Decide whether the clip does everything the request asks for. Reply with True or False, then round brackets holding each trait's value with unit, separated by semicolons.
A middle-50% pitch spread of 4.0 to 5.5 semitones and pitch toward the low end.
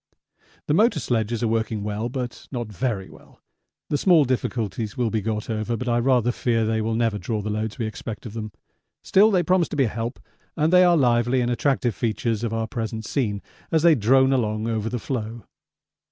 False (3.1 semitones; 115 Hz)